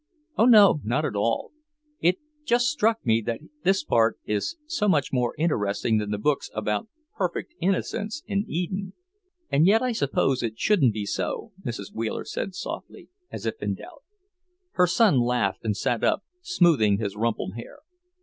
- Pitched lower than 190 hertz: Yes, medium, 140 Hz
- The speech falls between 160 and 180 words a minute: Yes, average, 170 wpm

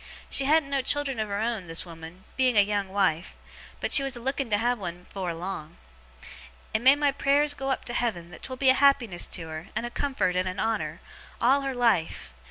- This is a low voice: No, high, 225 Hz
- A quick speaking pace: Yes, fast, 225 wpm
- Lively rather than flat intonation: Yes, wide, 6.7 semitones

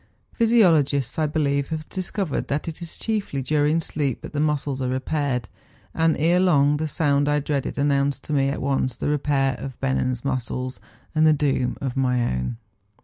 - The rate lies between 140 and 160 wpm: No, average, 185 wpm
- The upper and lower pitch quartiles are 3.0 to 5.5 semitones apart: No, narrow, 2.5 semitones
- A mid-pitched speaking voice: Yes, medium, 145 Hz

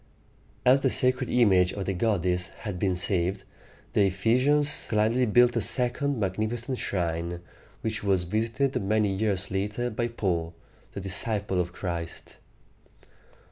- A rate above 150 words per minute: No, average, 140 wpm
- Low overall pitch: Yes, low, 105 Hz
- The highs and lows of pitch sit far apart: No, average, 4.4 semitones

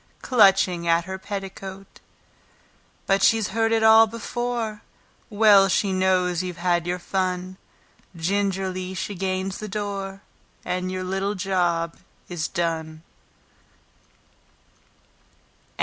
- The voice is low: No, high, 190 Hz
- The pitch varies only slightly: Yes, narrow, 2.1 semitones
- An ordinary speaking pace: No, slow, 105 wpm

